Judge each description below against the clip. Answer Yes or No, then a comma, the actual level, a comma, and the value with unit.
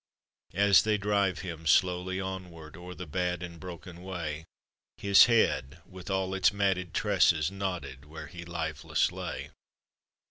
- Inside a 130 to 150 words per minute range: Yes, average, 140 wpm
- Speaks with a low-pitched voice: Yes, very low, 90 Hz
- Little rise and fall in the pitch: Yes, narrow, 2.3 semitones